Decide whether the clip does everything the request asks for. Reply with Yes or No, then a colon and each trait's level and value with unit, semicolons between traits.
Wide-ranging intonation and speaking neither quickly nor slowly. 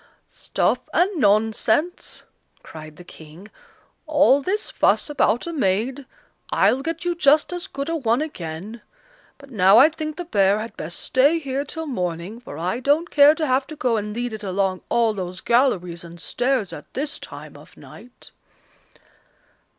Yes: wide, 7.2 semitones; average, 165 wpm